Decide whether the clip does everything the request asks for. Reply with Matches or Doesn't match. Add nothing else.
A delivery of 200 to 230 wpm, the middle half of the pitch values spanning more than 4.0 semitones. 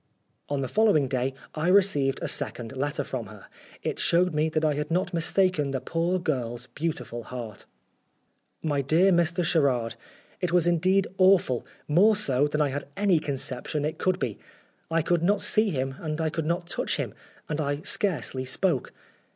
Doesn't match